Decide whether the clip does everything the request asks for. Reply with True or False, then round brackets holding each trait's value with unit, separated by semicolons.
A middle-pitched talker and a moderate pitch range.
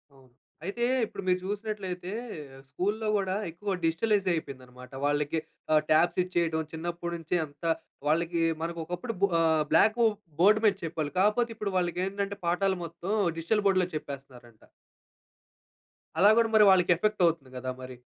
True (175 Hz; 4.0 semitones)